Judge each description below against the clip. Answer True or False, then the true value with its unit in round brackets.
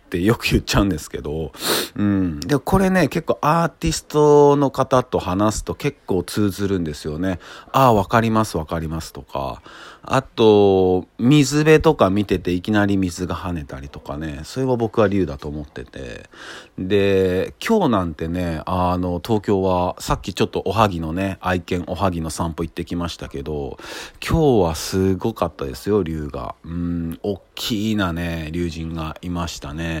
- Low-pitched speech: True (95 Hz)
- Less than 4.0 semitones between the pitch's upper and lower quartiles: False (4.7 semitones)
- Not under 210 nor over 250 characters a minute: False (325 characters per minute)